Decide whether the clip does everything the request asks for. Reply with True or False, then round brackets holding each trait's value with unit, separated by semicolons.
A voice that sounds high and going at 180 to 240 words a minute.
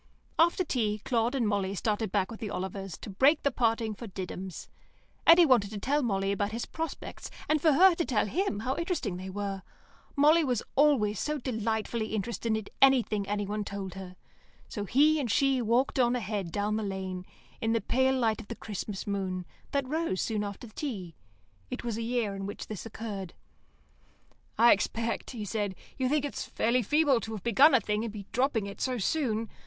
True (225 Hz; 190 wpm)